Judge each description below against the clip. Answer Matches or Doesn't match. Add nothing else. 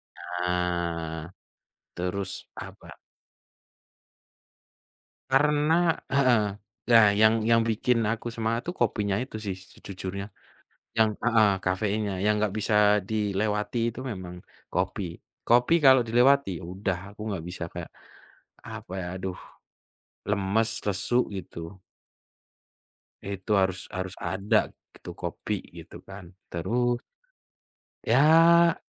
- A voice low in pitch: Matches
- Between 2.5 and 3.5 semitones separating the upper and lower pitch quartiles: Doesn't match